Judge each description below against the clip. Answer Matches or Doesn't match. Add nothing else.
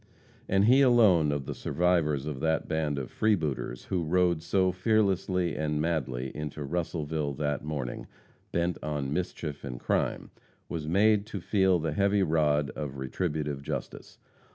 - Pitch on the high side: Doesn't match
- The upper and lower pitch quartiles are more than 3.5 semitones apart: Matches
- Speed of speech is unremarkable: Matches